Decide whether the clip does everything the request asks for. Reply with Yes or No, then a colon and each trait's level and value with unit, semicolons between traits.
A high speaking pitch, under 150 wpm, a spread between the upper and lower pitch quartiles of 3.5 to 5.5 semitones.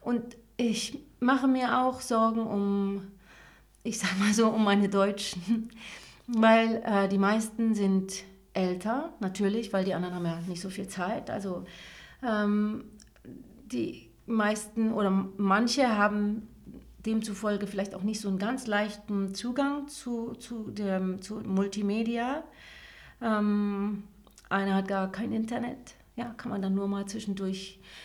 No: high, 210 Hz; average, 135 wpm; narrow, 2.6 semitones